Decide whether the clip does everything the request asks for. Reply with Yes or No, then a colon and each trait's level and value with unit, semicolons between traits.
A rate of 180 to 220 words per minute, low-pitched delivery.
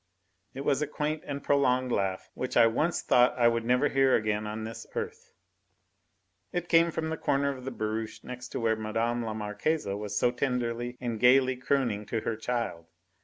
Yes: average, 190 wpm; low, 125 Hz